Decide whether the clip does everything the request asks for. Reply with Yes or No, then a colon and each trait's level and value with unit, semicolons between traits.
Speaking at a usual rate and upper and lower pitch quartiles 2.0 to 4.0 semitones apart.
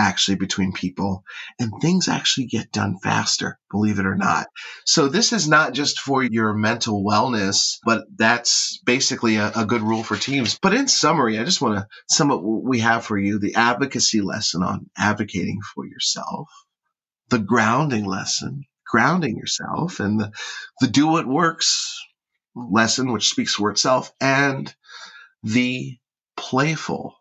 No: average, 155 wpm; average, 4.4 semitones